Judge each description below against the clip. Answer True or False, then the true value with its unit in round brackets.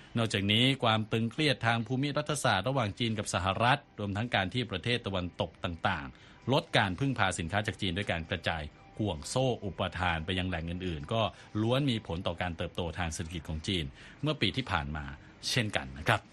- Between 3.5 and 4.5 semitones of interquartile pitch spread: False (4.9 semitones)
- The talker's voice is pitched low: True (105 Hz)